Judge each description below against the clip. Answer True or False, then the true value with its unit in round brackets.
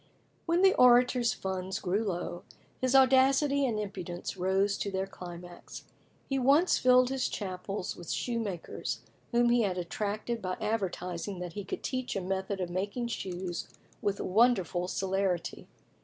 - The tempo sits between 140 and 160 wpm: True (145 wpm)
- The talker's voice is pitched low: False (200 Hz)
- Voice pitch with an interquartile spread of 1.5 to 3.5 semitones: False (5.0 semitones)